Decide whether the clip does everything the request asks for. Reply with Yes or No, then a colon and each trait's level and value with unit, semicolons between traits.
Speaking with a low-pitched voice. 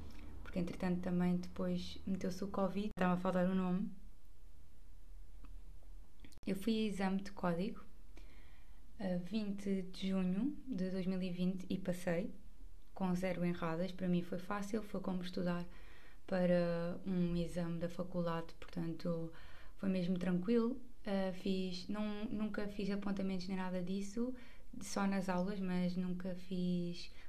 No: medium, 185 Hz